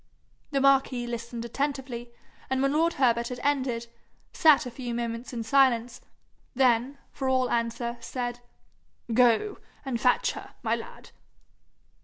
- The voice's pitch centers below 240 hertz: No, high, 245 Hz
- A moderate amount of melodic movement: No, narrow, 2.3 semitones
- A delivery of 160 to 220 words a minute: No, slow, 135 wpm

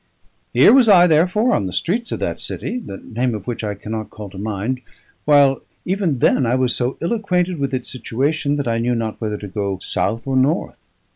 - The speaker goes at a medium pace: No, fast, 215 wpm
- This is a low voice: Yes, low, 130 Hz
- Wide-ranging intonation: Yes, wide, 7.2 semitones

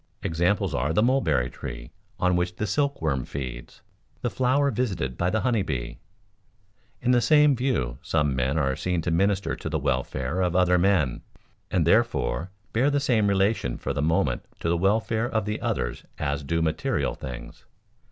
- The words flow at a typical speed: Yes, average, 170 wpm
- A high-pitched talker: No, very low, 90 Hz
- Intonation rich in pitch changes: Yes, wide, 7.7 semitones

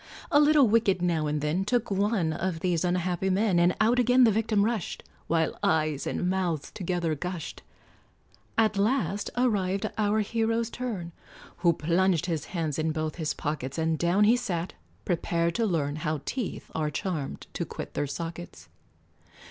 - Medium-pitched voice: Yes, medium, 180 Hz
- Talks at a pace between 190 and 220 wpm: No, average, 165 wpm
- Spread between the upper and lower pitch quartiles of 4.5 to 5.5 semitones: Yes, average, 4.8 semitones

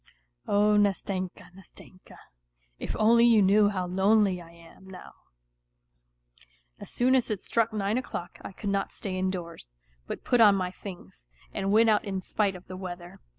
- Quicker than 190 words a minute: No, average, 165 wpm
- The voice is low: No, high, 195 Hz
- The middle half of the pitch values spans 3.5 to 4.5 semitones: No, narrow, 2.4 semitones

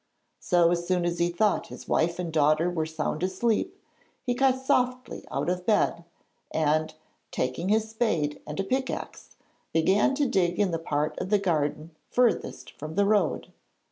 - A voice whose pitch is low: No, medium, 180 Hz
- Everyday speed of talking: Yes, average, 170 wpm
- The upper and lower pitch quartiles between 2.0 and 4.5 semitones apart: No, average, 5.1 semitones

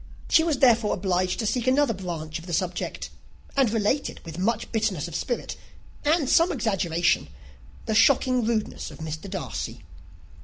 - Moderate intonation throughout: No, wide, 6.2 semitones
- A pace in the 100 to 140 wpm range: No, average, 155 wpm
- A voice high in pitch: Yes, high, 215 Hz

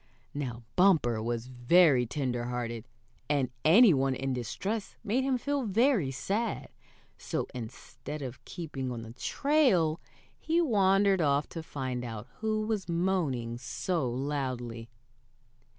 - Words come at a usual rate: No, slow, 125 wpm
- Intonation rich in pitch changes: Yes, wide, 8.0 semitones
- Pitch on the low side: No, medium, 145 Hz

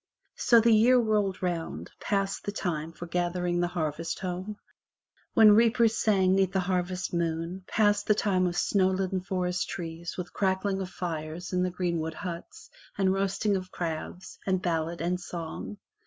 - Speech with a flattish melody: Yes, narrow, 2.2 semitones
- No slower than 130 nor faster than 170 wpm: Yes, average, 165 wpm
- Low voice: No, medium, 185 Hz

